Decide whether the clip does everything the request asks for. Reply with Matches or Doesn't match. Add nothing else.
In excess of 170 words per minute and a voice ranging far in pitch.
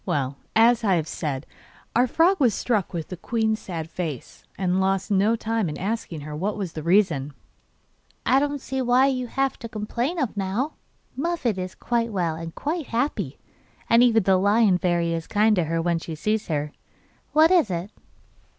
Matches